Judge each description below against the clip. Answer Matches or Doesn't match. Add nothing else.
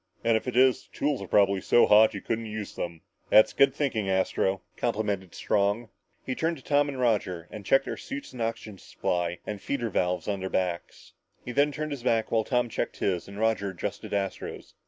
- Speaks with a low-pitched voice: Matches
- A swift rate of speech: Matches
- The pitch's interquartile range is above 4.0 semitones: Matches